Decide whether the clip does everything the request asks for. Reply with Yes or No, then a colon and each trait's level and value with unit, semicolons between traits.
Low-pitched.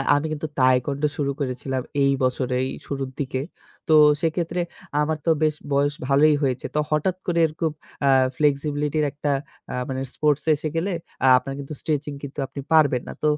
No: medium, 145 Hz